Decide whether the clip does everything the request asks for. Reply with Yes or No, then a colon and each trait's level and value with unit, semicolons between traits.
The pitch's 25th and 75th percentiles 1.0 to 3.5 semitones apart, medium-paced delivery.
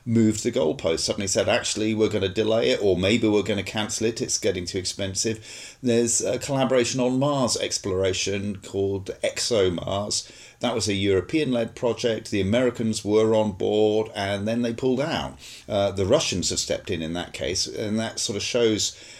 Yes: average, 2.9 semitones; average, 190 wpm